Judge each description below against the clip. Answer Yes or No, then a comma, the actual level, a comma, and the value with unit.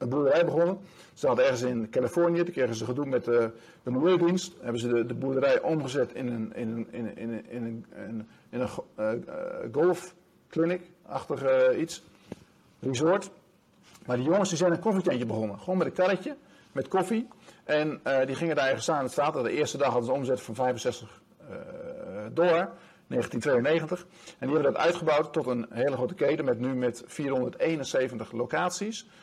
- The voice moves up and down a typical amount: No, wide, 6.9 semitones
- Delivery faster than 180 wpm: No, average, 160 wpm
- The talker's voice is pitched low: No, medium, 150 Hz